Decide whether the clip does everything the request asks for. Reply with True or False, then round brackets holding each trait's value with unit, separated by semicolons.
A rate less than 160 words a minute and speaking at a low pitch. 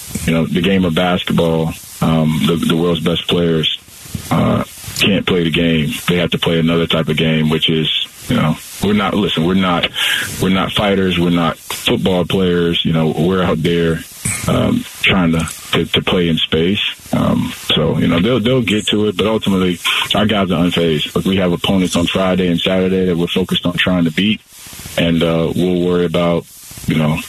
False (200 wpm; 85 Hz)